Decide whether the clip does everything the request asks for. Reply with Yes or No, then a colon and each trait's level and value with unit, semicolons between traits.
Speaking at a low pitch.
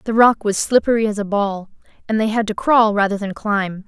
No: high, 210 Hz